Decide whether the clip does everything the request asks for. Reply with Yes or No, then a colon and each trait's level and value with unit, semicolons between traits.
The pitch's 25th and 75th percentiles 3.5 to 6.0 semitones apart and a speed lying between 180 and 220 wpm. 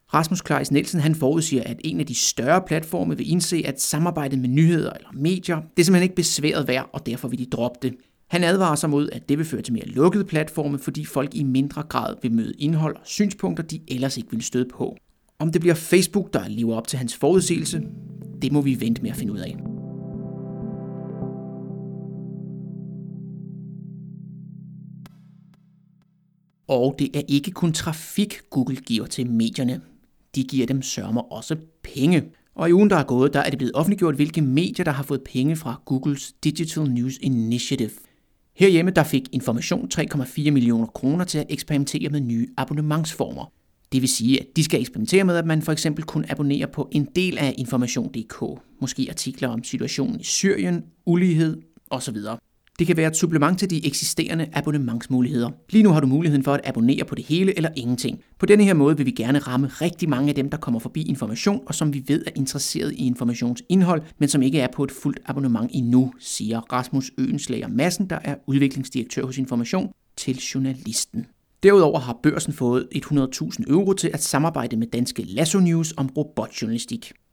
Yes: average, 4.6 semitones; average, 185 wpm